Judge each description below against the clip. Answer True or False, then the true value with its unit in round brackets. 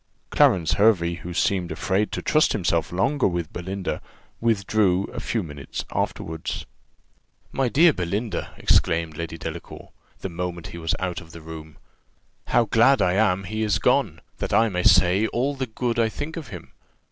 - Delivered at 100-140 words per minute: False (170 wpm)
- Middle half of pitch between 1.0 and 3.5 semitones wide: False (4.9 semitones)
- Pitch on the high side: False (95 Hz)